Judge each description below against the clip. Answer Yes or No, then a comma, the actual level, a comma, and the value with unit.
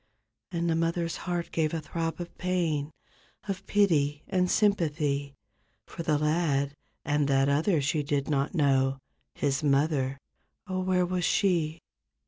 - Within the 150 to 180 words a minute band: No, slow, 135 wpm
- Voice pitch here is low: No, medium, 155 Hz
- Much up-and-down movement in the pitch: No, average, 3.7 semitones